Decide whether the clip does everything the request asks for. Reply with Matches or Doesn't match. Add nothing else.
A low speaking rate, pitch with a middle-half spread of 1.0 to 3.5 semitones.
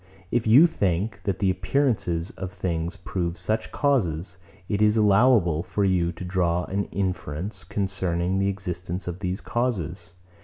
Doesn't match